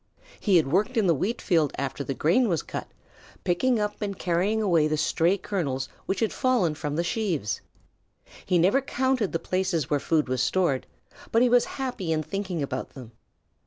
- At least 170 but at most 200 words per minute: Yes, average, 185 wpm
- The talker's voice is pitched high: No, medium, 180 Hz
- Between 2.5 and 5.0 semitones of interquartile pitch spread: No, wide, 5.6 semitones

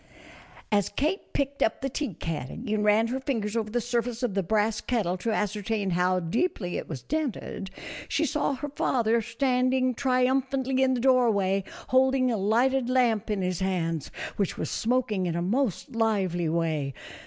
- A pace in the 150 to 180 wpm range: Yes, average, 175 wpm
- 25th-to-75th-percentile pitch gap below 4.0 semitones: No, average, 5.1 semitones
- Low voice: No, high, 225 Hz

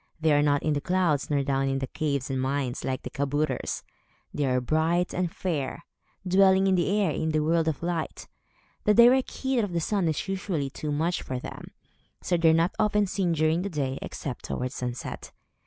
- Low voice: No, medium, 160 Hz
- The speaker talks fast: Yes, fast, 210 wpm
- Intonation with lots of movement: No, average, 4.5 semitones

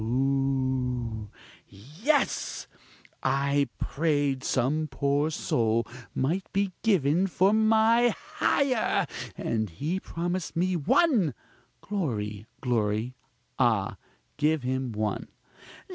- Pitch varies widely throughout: Yes, wide, 7.0 semitones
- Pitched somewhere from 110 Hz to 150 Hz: Yes, medium, 140 Hz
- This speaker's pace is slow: Yes, slow, 90 wpm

